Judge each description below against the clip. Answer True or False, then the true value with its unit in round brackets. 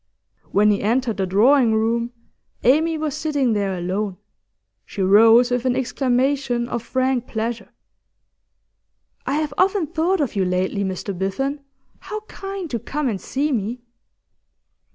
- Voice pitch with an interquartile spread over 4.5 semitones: True (5.4 semitones)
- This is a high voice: True (245 Hz)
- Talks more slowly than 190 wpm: True (140 wpm)